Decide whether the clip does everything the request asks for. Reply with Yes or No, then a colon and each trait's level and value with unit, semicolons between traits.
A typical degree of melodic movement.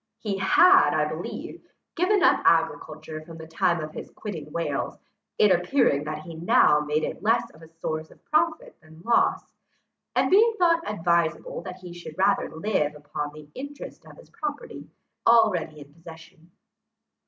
No: wide, 6.9 semitones